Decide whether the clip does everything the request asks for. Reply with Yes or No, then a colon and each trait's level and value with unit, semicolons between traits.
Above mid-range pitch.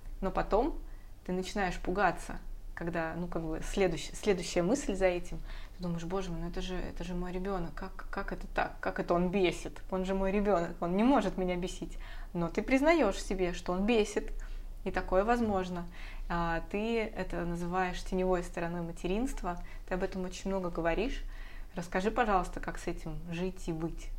No: medium, 180 Hz